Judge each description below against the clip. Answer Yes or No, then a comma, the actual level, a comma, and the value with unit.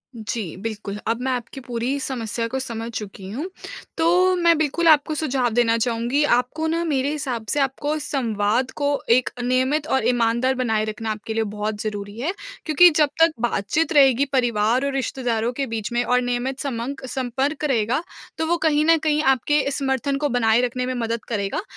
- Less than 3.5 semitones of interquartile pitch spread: No, average, 4.0 semitones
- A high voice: Yes, very high, 250 Hz